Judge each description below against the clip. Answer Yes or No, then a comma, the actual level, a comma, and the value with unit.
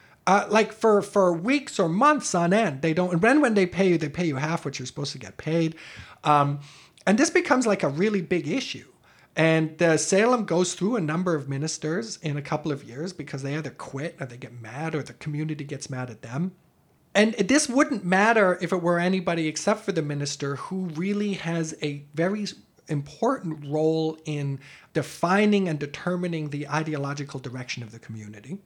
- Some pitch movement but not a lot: Yes, average, 4.8 semitones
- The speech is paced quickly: No, average, 195 wpm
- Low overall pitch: No, medium, 160 Hz